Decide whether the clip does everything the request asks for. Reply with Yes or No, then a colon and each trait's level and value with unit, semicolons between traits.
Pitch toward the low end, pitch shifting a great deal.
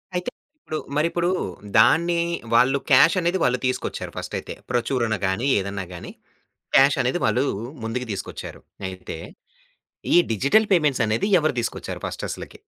Yes: low, 130 Hz; wide, 6.0 semitones